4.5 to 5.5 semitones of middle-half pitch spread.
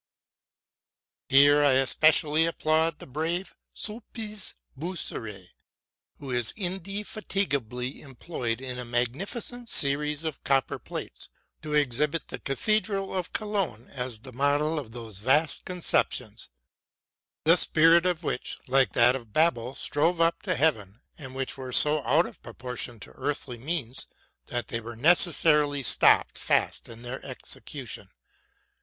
Yes: average, 5.1 semitones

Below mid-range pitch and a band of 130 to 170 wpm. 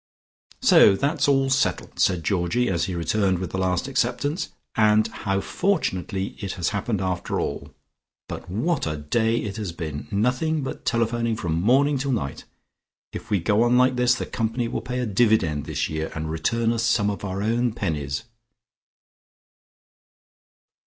Yes: low, 110 Hz; average, 165 wpm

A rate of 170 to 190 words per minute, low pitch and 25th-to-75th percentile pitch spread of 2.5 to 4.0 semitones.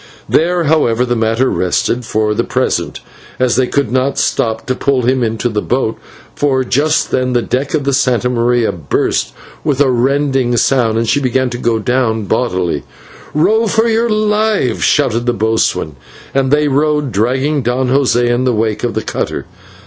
Yes: average, 180 wpm; low, 125 Hz; average, 3.5 semitones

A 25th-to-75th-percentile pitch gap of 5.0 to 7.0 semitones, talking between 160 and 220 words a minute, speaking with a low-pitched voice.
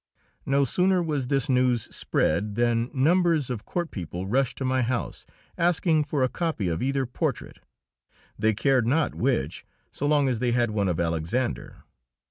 No: average, 4.4 semitones; average, 165 wpm; low, 130 Hz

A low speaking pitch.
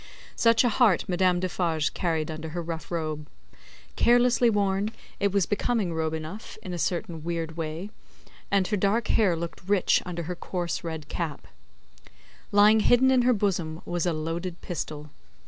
No: medium, 175 Hz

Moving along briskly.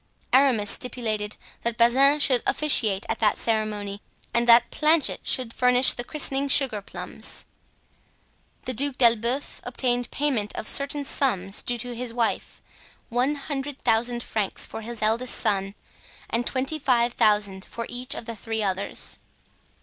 No: average, 145 wpm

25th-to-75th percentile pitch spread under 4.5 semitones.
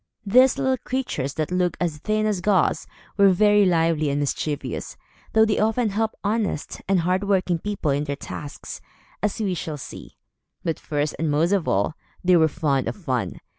No: wide, 5.5 semitones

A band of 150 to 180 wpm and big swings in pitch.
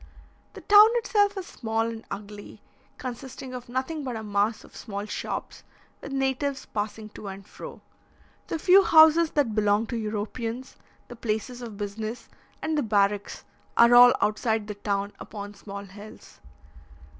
No: average, 155 wpm; average, 4.1 semitones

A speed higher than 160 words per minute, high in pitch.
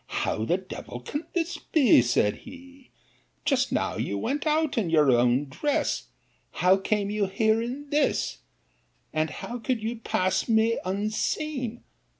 No: average, 150 wpm; high, 220 Hz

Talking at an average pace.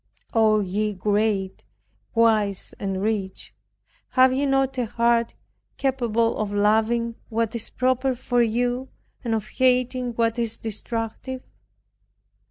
No: slow, 120 wpm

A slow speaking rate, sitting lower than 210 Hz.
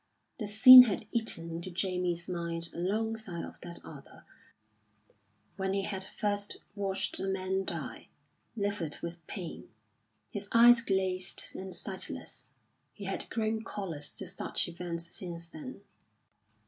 Yes: slow, 130 wpm; high, 190 Hz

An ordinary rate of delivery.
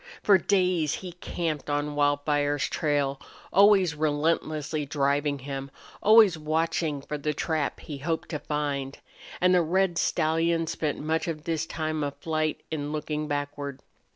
Yes: average, 145 wpm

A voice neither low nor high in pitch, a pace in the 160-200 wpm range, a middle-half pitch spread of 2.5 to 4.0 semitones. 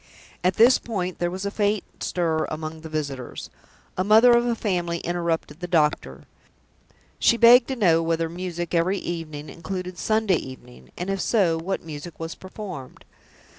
Yes: medium, 175 Hz; average, 165 wpm; average, 3.7 semitones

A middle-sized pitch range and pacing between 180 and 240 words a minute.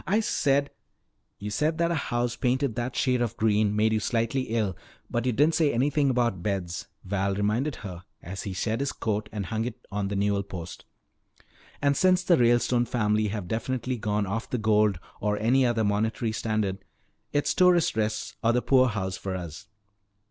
Yes: average, 3.8 semitones; average, 185 wpm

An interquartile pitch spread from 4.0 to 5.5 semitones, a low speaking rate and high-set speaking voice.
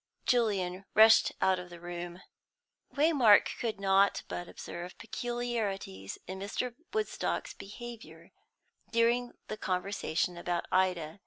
Yes: average, 4.6 semitones; slow, 110 wpm; high, 195 Hz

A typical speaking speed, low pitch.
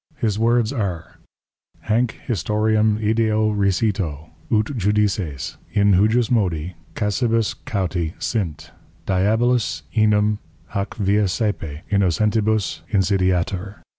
No: slow, 90 wpm; low, 105 Hz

